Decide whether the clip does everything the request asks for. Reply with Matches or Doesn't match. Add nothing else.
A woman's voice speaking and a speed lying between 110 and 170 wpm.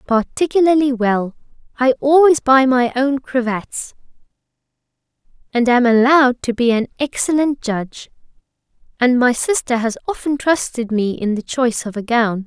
Matches